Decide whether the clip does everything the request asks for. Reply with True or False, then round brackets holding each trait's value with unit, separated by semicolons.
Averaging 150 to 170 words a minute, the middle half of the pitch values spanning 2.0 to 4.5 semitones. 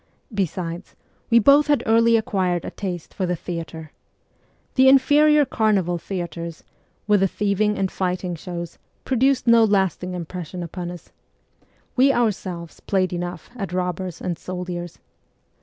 False (135 wpm; 4.0 semitones)